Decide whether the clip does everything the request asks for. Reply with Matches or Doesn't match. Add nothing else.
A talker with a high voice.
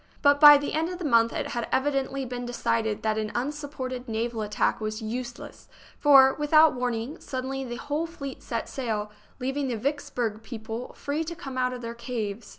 Matches